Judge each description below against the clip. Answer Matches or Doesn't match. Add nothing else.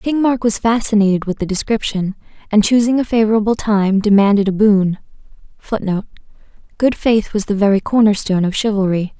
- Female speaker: Matches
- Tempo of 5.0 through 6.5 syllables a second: Matches